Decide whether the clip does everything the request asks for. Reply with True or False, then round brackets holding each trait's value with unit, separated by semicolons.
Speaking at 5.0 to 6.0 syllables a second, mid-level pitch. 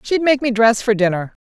False (5.5 syllables/s; 235 Hz)